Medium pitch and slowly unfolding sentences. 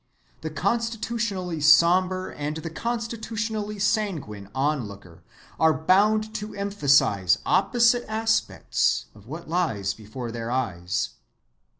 Yes: medium, 175 Hz; slow, 100 wpm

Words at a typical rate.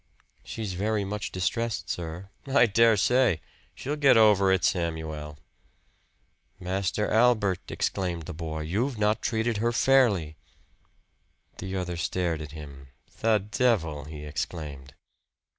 No: slow, 125 wpm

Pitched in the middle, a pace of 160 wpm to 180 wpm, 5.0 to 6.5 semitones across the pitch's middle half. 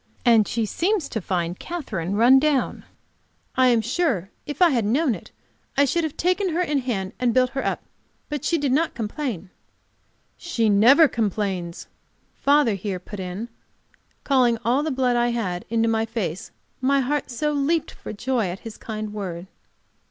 No: high, 240 Hz; average, 175 wpm; wide, 5.5 semitones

